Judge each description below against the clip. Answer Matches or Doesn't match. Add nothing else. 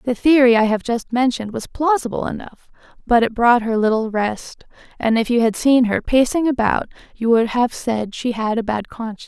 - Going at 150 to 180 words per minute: Doesn't match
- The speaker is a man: Doesn't match